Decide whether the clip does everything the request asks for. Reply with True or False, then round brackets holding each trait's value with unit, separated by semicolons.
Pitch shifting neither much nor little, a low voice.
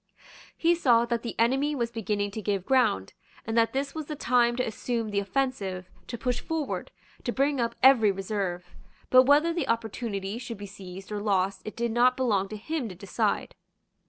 False (4.3 semitones; 230 Hz)